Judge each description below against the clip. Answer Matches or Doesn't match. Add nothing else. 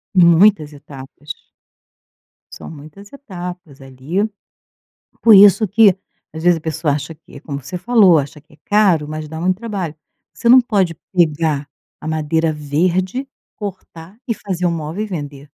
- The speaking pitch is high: Doesn't match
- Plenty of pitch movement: Doesn't match